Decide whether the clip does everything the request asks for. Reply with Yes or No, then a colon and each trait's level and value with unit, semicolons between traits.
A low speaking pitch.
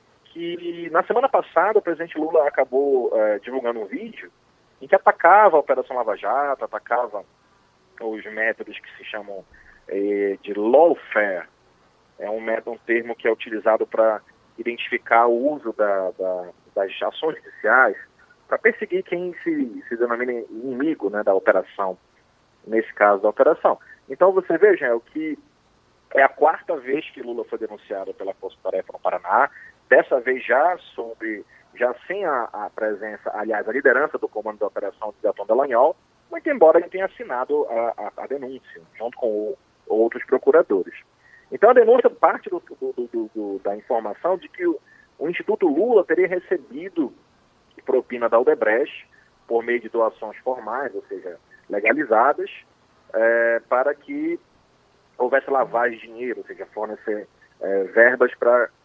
No: medium, 175 Hz